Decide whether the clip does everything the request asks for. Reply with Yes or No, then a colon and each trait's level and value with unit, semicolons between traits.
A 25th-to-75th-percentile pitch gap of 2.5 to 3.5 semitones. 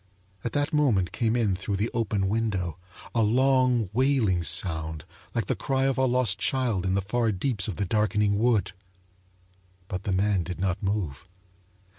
No: average, 4.6 semitones